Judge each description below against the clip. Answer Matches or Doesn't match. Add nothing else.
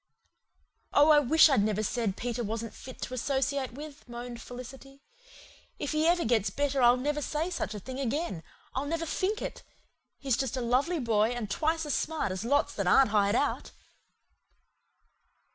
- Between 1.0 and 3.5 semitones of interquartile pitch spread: Doesn't match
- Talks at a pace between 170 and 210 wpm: Matches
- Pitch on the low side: Doesn't match